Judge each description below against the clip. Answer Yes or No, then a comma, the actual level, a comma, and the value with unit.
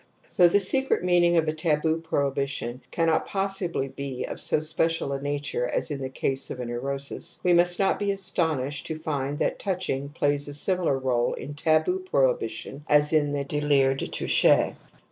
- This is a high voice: No, medium, 150 Hz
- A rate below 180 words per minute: No, average, 185 wpm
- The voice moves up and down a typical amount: Yes, average, 4.0 semitones